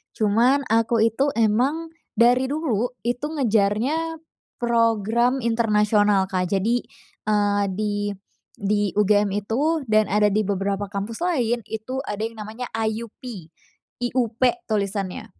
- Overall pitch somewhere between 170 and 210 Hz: No, high, 225 Hz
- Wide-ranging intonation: No, average, 2.8 semitones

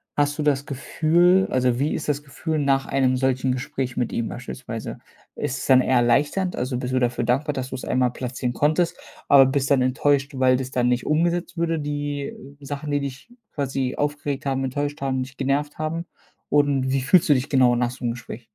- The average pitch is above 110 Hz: Yes, low, 135 Hz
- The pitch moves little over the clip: Yes, narrow, 2.3 semitones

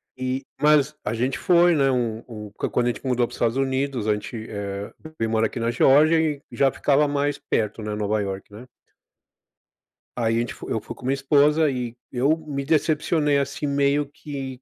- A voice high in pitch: No, low, 135 Hz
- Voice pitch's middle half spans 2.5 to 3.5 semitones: No, average, 4.0 semitones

